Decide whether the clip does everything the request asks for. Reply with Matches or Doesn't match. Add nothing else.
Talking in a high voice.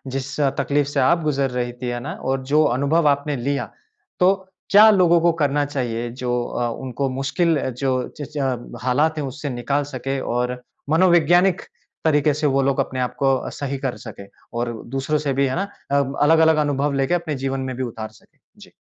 Doesn't match